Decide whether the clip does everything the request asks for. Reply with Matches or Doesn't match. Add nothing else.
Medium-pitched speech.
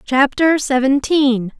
Doesn't match